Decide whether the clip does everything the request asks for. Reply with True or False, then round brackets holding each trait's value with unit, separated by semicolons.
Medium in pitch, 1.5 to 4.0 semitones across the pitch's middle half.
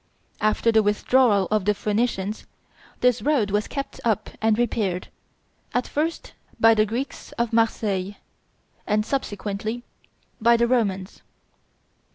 False (220 Hz; 2.6 semitones)